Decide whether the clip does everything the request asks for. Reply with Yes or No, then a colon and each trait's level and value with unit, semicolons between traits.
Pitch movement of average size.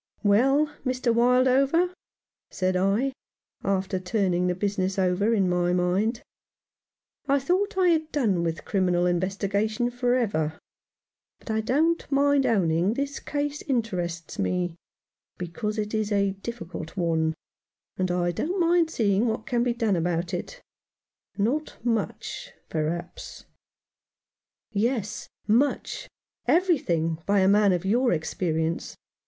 No: wide, 6.0 semitones